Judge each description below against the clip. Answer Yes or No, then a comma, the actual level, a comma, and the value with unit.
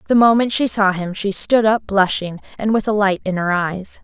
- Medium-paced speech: No, fast, 240 wpm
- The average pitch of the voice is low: No, high, 205 Hz